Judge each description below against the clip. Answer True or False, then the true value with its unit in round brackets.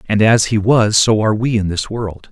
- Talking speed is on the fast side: True (260 wpm)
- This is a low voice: True (110 Hz)